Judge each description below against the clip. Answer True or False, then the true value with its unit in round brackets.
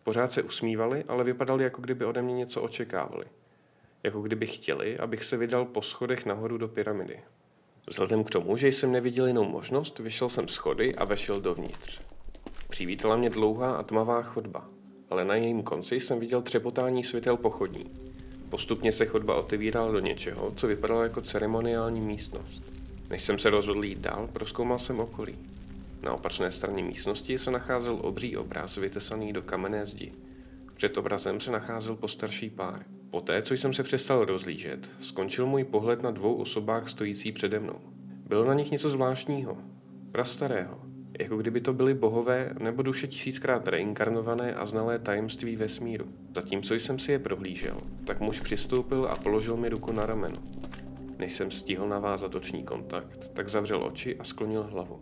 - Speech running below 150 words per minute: False (165 wpm)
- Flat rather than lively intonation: False (4.6 semitones)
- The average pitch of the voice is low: True (110 Hz)